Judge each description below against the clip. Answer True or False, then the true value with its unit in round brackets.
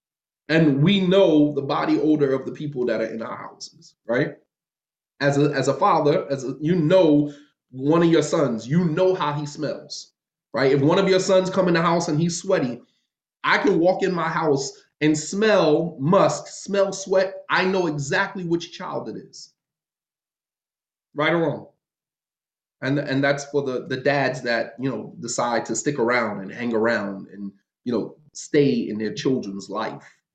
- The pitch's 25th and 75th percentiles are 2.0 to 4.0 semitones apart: False (4.6 semitones)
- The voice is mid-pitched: True (150 Hz)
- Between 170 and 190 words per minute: True (180 wpm)